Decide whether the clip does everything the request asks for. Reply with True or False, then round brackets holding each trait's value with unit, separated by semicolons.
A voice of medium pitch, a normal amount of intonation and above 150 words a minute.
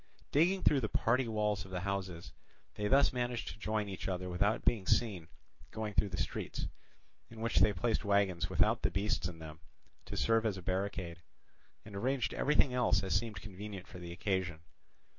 False (100 Hz; 3.5 semitones; 185 wpm)